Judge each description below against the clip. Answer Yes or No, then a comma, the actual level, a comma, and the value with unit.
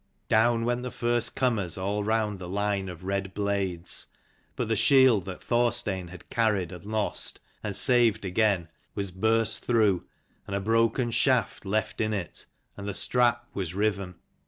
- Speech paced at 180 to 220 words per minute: No, average, 160 wpm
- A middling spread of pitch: Yes, average, 3.1 semitones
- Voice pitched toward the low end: Yes, low, 105 Hz